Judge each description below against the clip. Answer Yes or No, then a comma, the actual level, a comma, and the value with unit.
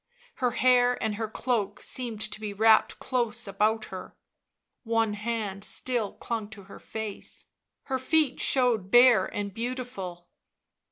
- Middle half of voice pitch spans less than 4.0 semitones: Yes, average, 3.1 semitones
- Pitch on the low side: No, high, 220 Hz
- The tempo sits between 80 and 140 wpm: Yes, slow, 135 wpm